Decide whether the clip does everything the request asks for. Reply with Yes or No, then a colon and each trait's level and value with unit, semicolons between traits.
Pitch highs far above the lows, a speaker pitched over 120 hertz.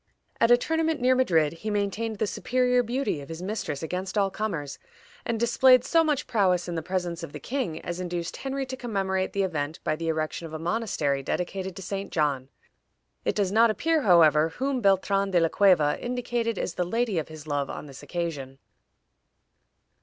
Yes: wide, 6.2 semitones; high, 190 Hz